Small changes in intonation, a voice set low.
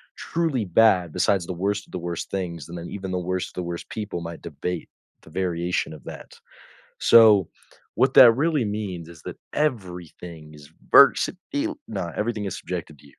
No: average, 4.2 semitones; very low, 90 Hz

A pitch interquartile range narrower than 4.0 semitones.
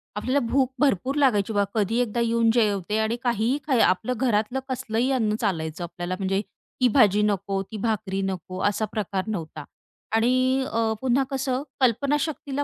No: average, 4.3 semitones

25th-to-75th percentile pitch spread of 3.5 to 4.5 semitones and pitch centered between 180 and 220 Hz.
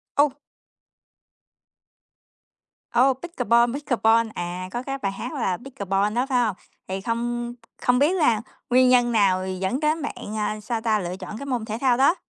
No: average, 3.8 semitones; high, 240 Hz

